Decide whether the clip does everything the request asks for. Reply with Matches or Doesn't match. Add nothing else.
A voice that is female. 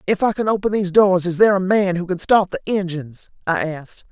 Matches